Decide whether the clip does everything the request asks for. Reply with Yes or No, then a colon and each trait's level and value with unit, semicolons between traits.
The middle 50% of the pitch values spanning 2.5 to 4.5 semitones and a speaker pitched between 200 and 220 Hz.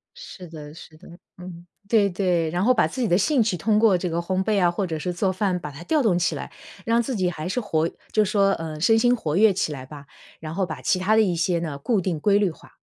No: average, 4.2 semitones; medium, 185 Hz